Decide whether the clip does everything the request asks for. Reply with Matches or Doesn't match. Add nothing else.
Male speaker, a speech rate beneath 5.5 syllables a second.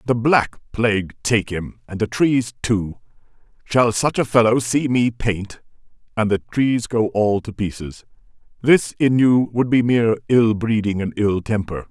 Matches